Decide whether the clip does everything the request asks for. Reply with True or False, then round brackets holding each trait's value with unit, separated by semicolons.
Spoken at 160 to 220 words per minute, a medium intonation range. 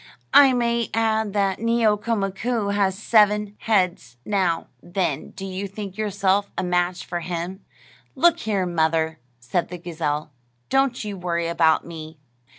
False (145 wpm; 3.7 semitones)